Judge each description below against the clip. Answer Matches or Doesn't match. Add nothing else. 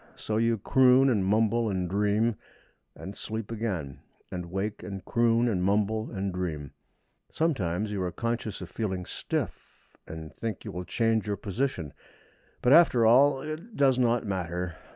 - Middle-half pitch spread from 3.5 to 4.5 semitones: Matches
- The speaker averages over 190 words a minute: Doesn't match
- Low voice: Matches